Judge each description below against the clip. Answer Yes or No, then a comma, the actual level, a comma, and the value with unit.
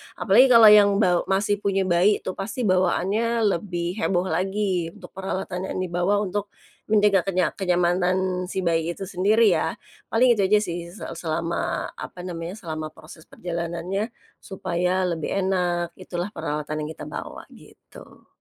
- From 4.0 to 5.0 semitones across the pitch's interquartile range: No, narrow, 2.5 semitones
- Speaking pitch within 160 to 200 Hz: Yes, medium, 185 Hz